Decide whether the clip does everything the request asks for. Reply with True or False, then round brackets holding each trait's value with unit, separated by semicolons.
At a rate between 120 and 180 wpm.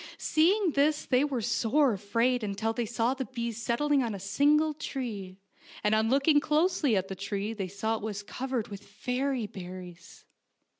True (170 wpm)